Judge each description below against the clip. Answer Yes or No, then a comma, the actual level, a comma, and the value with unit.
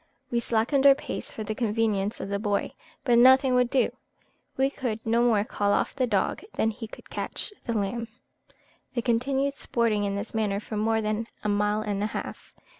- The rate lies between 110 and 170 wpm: No, average, 195 wpm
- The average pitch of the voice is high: Yes, high, 225 Hz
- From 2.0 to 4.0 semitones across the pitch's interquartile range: Yes, average, 2.8 semitones